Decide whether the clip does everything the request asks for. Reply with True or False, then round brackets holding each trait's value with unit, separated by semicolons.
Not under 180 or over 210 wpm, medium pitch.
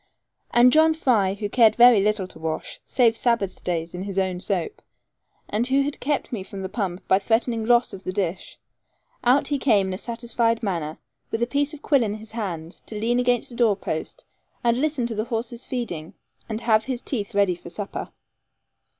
False (200 wpm; 225 Hz)